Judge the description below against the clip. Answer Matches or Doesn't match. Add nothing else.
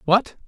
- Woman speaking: Doesn't match